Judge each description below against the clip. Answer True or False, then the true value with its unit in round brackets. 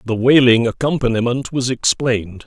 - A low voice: True (120 Hz)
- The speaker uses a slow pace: True (120 wpm)